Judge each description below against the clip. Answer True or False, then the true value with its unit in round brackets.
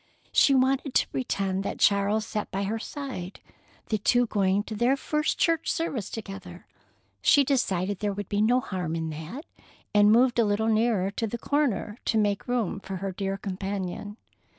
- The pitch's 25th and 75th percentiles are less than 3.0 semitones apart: False (3.9 semitones)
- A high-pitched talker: True (210 Hz)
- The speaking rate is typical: True (175 wpm)